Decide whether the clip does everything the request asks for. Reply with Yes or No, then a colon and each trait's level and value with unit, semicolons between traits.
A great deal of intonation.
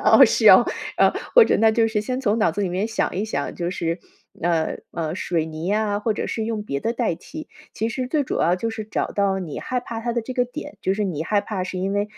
No: average, 4.2 semitones